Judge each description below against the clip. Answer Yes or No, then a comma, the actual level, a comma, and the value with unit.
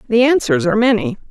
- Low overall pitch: No, very high, 250 Hz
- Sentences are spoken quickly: No, average, 185 wpm